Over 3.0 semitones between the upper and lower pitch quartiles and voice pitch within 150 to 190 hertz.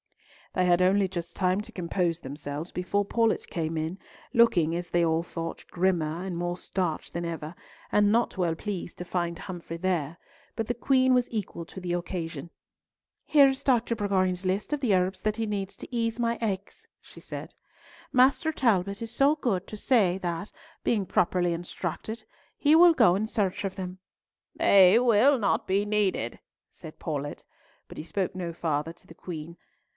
Yes: average, 4.2 semitones; medium, 185 Hz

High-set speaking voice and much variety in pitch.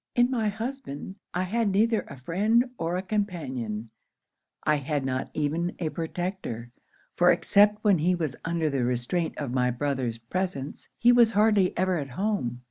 No: medium, 175 Hz; wide, 7.5 semitones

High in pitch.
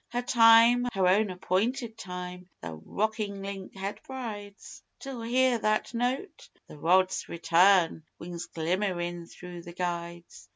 Yes: high, 195 Hz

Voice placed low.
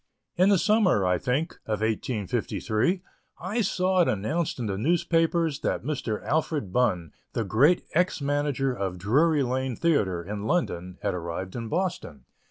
Yes: low, 130 Hz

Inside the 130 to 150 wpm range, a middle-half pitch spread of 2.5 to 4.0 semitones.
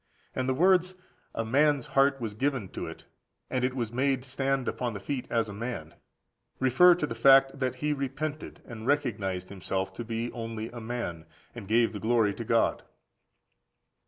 No: average, 180 wpm; average, 3.5 semitones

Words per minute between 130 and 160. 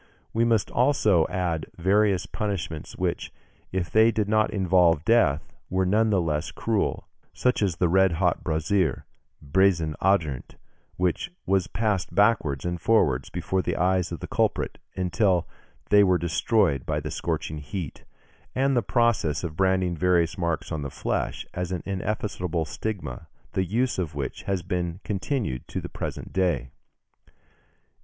Yes: average, 150 wpm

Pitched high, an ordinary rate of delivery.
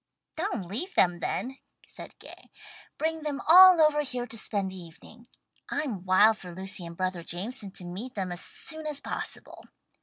Yes: high, 220 Hz; average, 175 wpm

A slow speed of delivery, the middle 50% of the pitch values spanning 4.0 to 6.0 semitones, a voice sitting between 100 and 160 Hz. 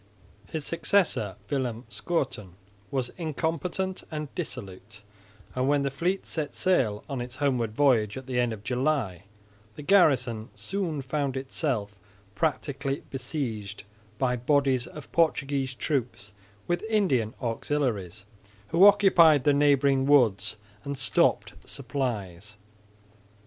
Yes: slow, 120 wpm; average, 4.7 semitones; low, 135 Hz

